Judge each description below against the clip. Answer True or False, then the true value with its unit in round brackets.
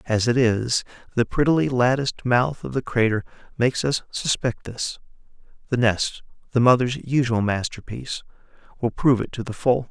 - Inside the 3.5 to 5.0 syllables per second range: False (5.2 syllables/s)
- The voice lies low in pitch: True (125 Hz)